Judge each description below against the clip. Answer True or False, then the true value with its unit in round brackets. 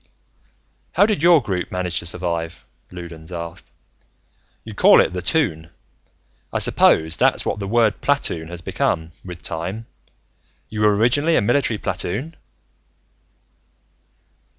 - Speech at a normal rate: False (130 wpm)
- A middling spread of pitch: False (5.9 semitones)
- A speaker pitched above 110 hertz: False (90 Hz)